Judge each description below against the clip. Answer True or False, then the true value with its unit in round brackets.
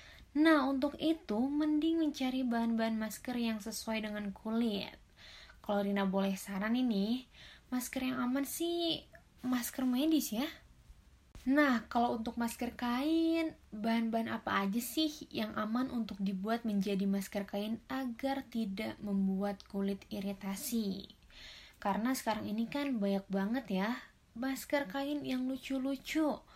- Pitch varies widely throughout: False (4.5 semitones)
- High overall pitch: True (235 Hz)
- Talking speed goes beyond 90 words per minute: True (125 wpm)